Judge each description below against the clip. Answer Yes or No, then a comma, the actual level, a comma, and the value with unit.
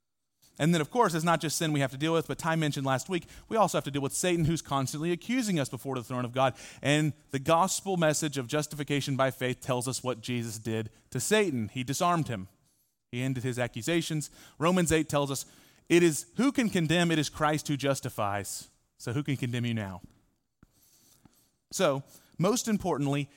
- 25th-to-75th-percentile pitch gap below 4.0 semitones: No, average, 4.3 semitones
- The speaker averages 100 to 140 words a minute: No, fast, 205 wpm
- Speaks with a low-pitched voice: No, medium, 145 Hz